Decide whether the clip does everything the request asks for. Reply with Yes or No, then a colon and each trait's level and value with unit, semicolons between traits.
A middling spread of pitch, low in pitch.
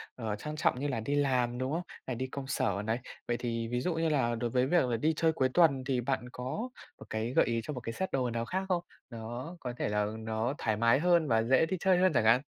Yes: average, 4.6 semitones; low, 125 Hz